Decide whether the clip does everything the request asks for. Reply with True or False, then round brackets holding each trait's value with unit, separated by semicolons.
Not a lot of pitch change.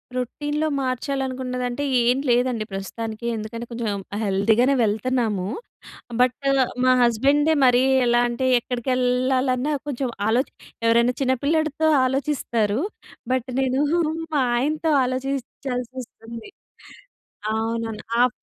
True (2.3 semitones)